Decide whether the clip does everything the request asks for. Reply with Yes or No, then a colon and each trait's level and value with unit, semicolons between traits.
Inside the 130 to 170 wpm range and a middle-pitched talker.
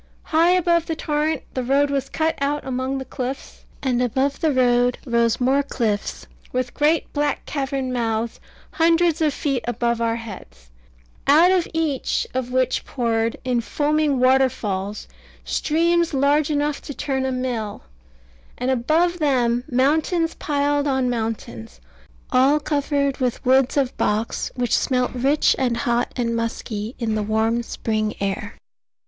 No: average, 145 wpm; very high, 260 Hz